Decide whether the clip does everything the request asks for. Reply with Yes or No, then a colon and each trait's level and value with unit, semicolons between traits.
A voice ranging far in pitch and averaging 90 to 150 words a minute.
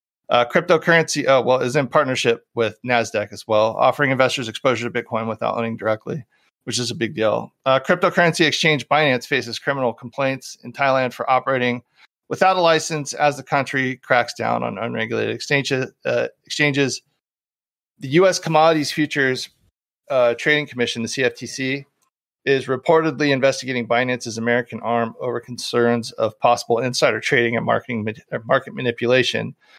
No: average, 3.4 semitones; average, 145 wpm